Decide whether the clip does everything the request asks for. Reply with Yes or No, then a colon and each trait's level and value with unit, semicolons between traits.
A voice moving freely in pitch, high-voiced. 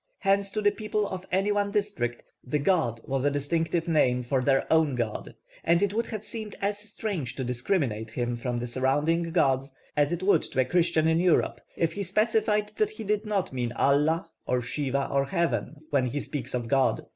No: wide, 7.3 semitones; medium, 160 Hz